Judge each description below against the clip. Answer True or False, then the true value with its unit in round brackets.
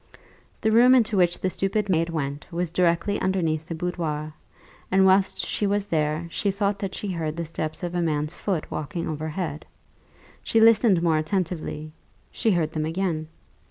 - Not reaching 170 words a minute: False (175 wpm)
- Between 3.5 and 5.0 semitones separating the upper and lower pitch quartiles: True (3.8 semitones)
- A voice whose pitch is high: False (175 Hz)